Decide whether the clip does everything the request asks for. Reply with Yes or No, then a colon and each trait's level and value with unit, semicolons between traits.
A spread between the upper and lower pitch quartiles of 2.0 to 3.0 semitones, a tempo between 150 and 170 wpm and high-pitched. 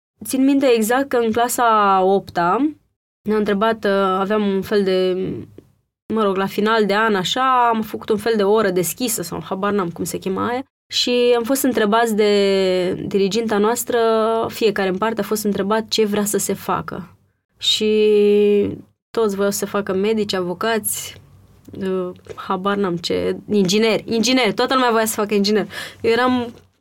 Yes: average, 2.7 semitones; average, 165 wpm; high, 210 Hz